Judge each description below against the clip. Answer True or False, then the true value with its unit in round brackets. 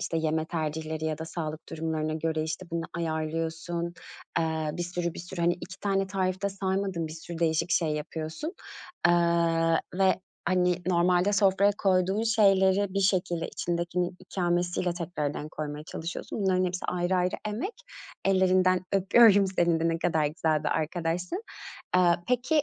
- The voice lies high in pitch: False (175 Hz)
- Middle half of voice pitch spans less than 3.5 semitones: True (2.6 semitones)